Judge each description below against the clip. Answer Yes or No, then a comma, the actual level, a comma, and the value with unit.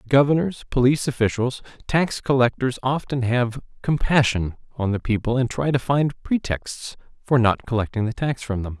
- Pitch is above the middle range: No, low, 125 Hz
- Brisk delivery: No, average, 155 wpm